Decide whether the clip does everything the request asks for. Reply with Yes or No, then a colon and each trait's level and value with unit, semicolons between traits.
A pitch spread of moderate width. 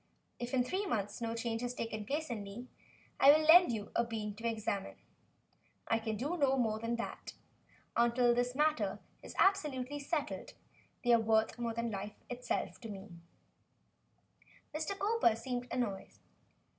Yes: average, 3.5 semitones